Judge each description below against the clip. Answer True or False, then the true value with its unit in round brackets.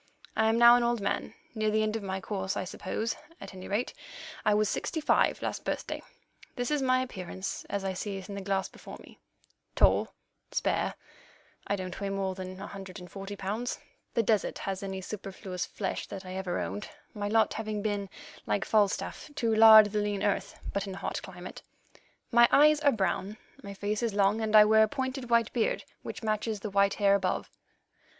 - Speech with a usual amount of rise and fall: False (2.3 semitones)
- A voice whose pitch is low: False (205 Hz)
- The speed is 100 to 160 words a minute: False (200 wpm)